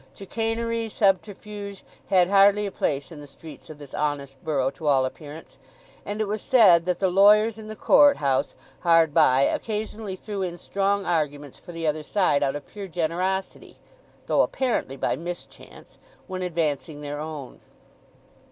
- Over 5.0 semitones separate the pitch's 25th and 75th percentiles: Yes, wide, 5.5 semitones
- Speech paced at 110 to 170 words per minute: Yes, average, 160 wpm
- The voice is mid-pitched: Yes, medium, 175 Hz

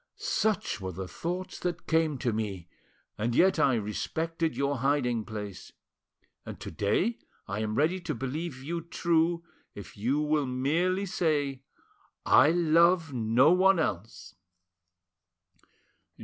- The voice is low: No, medium, 145 Hz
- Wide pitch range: Yes, wide, 7.1 semitones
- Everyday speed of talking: No, slow, 130 wpm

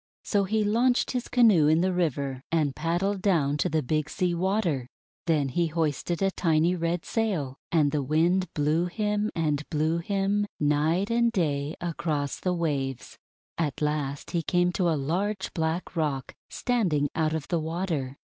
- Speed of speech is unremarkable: Yes, average, 170 wpm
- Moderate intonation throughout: Yes, average, 4.1 semitones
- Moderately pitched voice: Yes, medium, 165 Hz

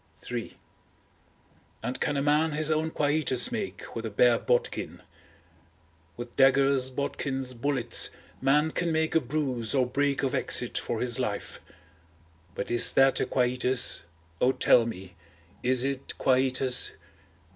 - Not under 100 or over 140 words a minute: Yes, slow, 135 wpm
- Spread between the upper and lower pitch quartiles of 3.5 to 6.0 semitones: No, average, 2.7 semitones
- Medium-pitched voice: No, low, 130 Hz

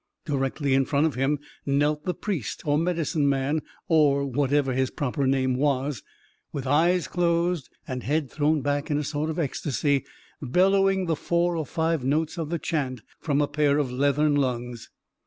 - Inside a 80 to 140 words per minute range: No, average, 175 wpm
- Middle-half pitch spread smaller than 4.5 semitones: Yes, average, 3.0 semitones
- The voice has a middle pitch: Yes, medium, 145 Hz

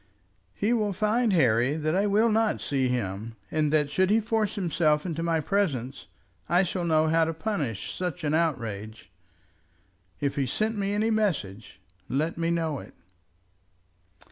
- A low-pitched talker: No, medium, 165 Hz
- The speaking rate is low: No, average, 160 wpm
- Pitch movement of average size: No, wide, 6.5 semitones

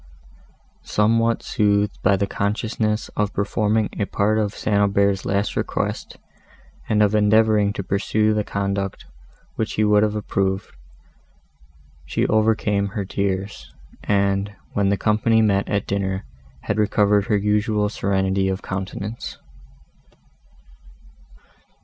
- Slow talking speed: Yes, slow, 120 wpm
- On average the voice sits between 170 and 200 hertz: No, low, 100 Hz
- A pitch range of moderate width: No, narrow, 1.4 semitones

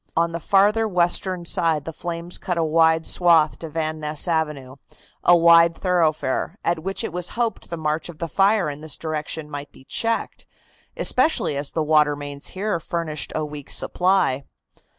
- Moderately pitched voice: Yes, medium, 165 Hz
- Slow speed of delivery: No, average, 175 wpm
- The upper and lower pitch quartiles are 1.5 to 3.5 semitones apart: Yes, narrow, 2.6 semitones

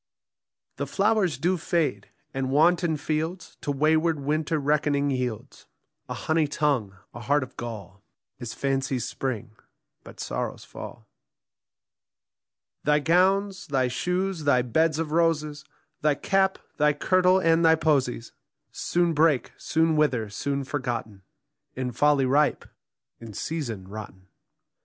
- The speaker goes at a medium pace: No, slow, 125 wpm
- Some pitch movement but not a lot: Yes, average, 4.2 semitones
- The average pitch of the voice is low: No, medium, 150 Hz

